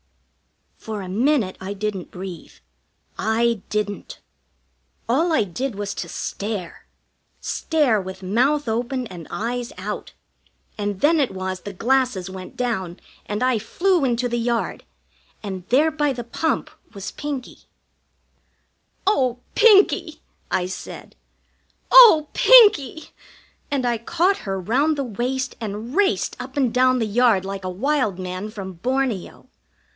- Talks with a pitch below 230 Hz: No, high, 235 Hz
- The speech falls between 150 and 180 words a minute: No, slow, 135 wpm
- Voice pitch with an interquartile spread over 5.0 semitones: Yes, wide, 5.5 semitones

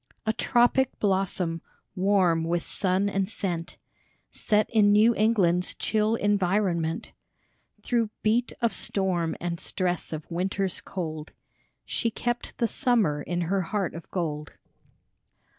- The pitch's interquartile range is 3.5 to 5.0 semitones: Yes, average, 3.9 semitones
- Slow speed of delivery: Yes, slow, 125 wpm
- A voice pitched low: No, high, 190 Hz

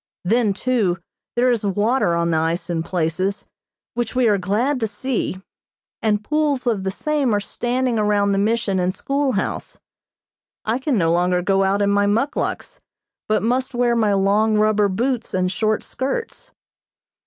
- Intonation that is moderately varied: Yes, average, 4.2 semitones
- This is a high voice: Yes, high, 210 Hz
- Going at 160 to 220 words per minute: Yes, average, 165 wpm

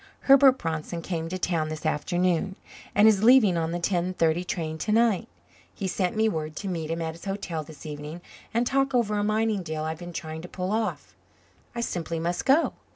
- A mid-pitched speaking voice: Yes, medium, 175 Hz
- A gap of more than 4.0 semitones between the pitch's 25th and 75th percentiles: Yes, average, 4.8 semitones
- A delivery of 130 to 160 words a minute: No, fast, 205 wpm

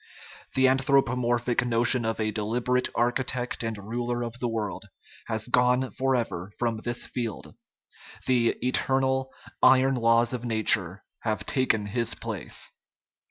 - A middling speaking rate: No, slow, 125 wpm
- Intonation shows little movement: Yes, narrow, 2.0 semitones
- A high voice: No, low, 120 Hz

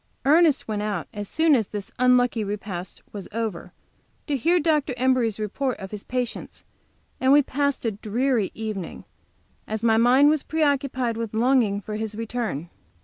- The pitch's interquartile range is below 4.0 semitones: No, average, 4.3 semitones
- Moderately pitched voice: No, high, 230 Hz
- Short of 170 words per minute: Yes, average, 160 wpm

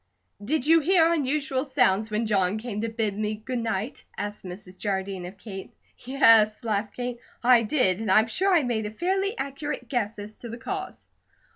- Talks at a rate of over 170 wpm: Yes, average, 185 wpm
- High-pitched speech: Yes, high, 225 Hz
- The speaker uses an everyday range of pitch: Yes, average, 4.8 semitones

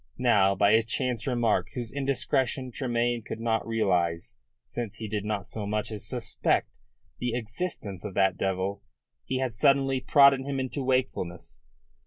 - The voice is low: Yes, low, 115 Hz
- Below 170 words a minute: Yes, average, 155 wpm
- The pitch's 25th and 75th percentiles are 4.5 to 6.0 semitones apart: No, average, 4.1 semitones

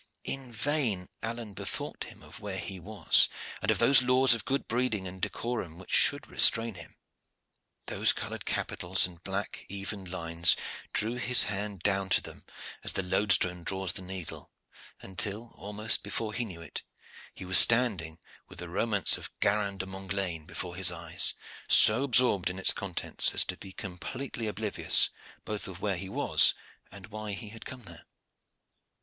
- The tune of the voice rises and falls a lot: No, average, 3.5 semitones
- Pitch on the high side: No, low, 100 Hz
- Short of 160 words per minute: No, average, 165 wpm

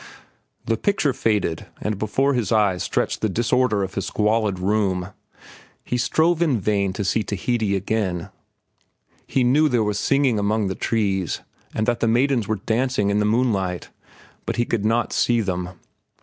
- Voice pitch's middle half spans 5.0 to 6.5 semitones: No, average, 3.4 semitones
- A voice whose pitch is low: Yes, low, 110 Hz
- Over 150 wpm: Yes, average, 165 wpm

